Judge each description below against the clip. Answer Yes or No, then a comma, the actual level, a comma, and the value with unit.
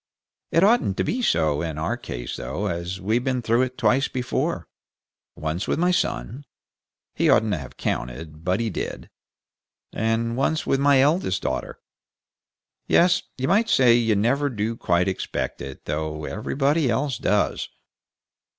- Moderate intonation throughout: No, wide, 8.2 semitones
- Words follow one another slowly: No, average, 150 wpm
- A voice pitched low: Yes, low, 115 Hz